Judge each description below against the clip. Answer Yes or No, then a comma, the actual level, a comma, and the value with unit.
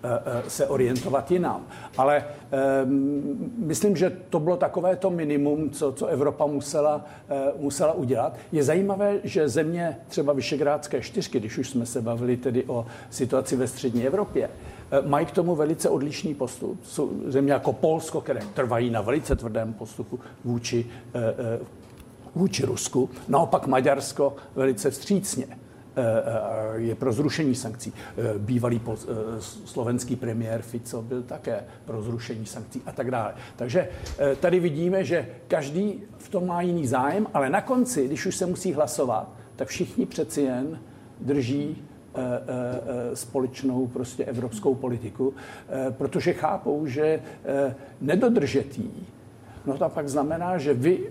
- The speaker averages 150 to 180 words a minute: No, average, 135 wpm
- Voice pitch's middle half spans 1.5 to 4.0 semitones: No, average, 4.4 semitones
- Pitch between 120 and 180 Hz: Yes, medium, 140 Hz